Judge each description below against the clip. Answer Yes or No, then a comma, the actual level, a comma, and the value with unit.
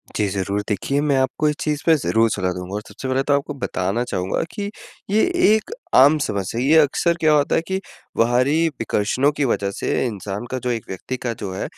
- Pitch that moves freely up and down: Yes, wide, 6.4 semitones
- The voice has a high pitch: No, low, 125 Hz